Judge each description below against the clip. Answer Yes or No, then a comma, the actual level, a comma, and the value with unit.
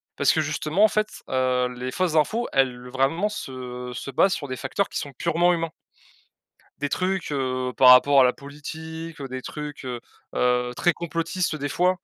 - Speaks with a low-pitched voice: No, medium, 145 Hz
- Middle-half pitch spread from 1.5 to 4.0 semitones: No, average, 4.6 semitones